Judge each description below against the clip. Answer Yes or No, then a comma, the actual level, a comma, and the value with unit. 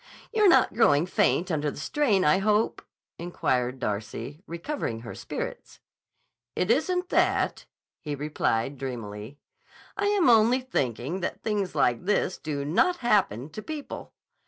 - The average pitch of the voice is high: No, medium, 170 Hz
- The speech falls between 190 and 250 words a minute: No, slow, 135 wpm